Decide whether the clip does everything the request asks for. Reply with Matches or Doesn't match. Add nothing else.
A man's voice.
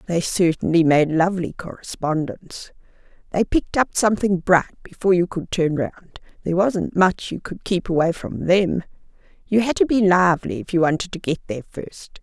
Doesn't match